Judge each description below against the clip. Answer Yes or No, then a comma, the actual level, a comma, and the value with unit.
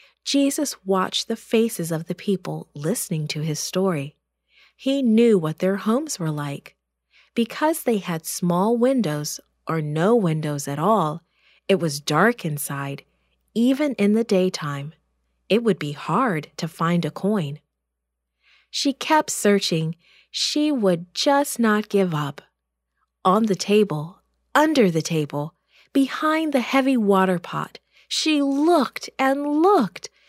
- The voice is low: No, high, 190 Hz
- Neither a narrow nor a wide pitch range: No, wide, 7.6 semitones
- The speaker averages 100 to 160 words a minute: Yes, slow, 135 wpm